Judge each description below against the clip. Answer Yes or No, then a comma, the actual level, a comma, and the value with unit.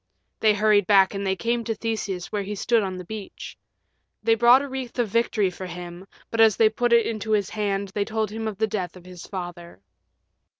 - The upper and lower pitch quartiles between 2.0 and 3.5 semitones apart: Yes, average, 2.9 semitones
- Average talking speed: No, fast, 220 wpm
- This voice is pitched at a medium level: No, high, 210 Hz